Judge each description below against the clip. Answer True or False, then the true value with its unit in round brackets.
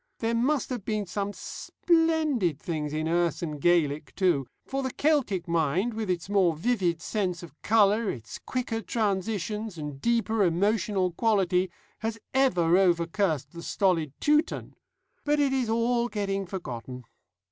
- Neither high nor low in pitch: False (195 Hz)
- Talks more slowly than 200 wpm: True (145 wpm)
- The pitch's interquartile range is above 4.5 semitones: True (5.2 semitones)